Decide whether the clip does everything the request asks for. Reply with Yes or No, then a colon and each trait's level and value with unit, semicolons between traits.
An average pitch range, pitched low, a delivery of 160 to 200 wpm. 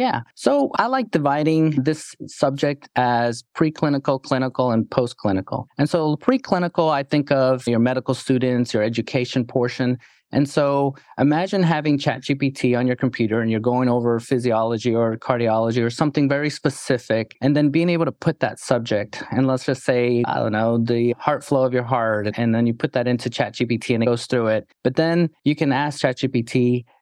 Yes: average, 3.6 semitones; low, 130 Hz; average, 180 wpm